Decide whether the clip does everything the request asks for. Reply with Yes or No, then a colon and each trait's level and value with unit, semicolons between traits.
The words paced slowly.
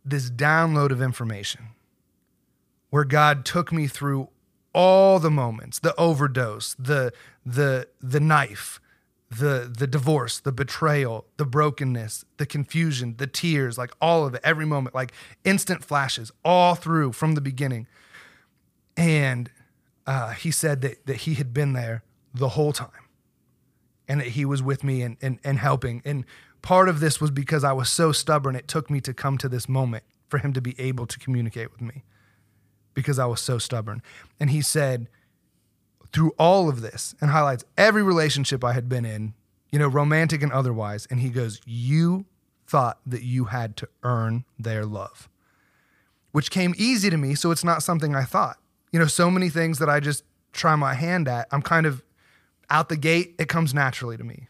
No: average, 180 wpm